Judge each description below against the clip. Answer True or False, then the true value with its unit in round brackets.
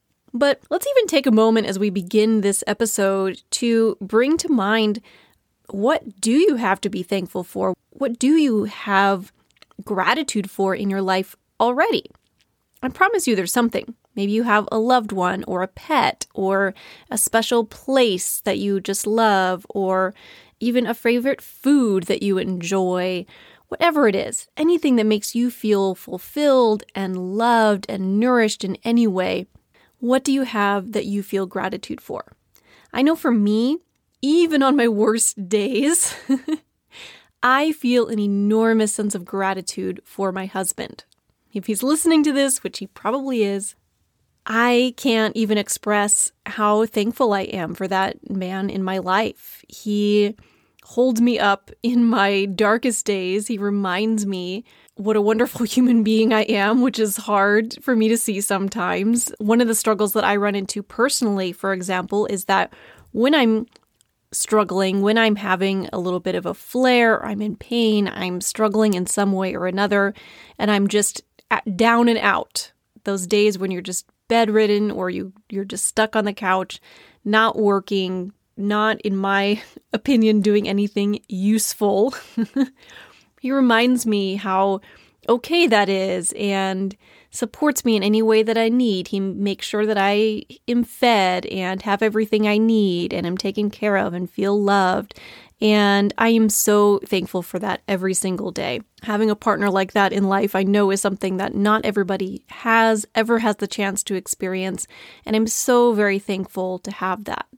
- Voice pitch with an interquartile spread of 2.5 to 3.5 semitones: True (2.9 semitones)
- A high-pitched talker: True (210 Hz)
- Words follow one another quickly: False (165 wpm)